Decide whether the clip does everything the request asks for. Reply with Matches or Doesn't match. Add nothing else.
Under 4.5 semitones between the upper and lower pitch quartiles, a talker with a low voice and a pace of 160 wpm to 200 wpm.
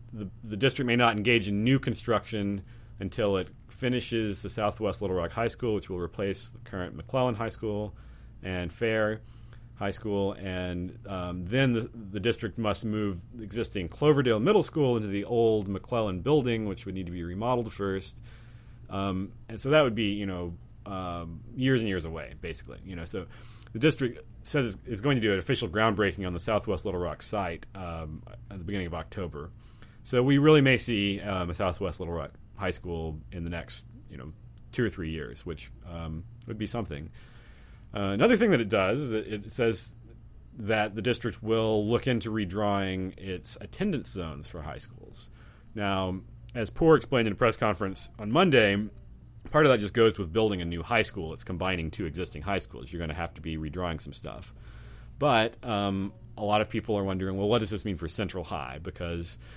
Matches